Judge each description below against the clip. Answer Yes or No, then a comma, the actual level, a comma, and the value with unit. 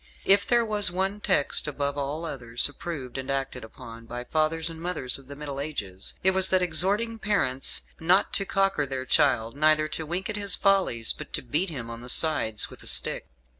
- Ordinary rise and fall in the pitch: No, wide, 6.4 semitones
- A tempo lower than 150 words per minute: No, fast, 205 wpm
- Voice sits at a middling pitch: Yes, medium, 155 Hz